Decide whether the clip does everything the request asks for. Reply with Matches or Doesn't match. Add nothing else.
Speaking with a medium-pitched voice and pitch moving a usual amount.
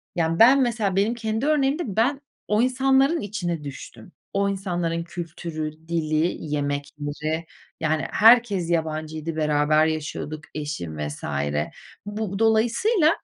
Doesn't match